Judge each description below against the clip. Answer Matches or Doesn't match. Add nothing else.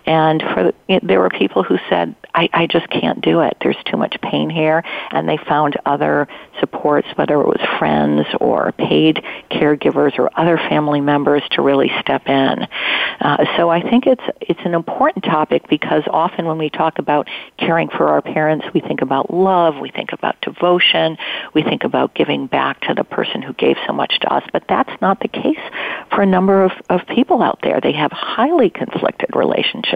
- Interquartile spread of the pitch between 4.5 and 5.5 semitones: Doesn't match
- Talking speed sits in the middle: Matches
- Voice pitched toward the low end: Doesn't match